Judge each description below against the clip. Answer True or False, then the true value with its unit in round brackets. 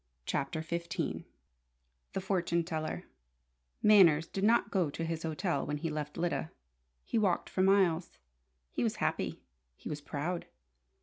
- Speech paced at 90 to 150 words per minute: True (140 wpm)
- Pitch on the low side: False (170 Hz)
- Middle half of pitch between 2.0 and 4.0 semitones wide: True (3.3 semitones)